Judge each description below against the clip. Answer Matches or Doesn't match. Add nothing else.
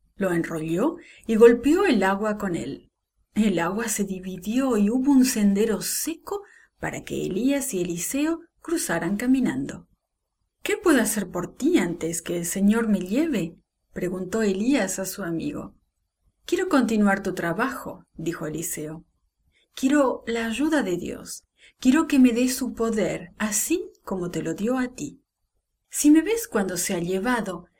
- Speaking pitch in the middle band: Doesn't match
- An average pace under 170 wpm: Matches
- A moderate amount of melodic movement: Doesn't match